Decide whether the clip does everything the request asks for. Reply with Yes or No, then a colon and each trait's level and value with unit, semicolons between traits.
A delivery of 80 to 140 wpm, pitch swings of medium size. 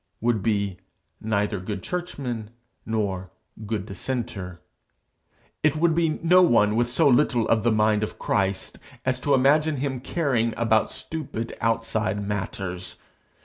Yes: slow, 135 wpm; average, 4.4 semitones